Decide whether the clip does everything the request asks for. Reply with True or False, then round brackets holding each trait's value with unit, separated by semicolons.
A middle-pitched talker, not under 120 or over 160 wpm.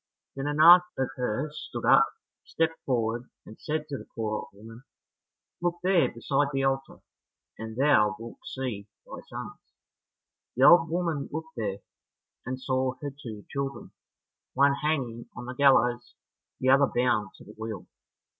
False (130 Hz; 155 wpm)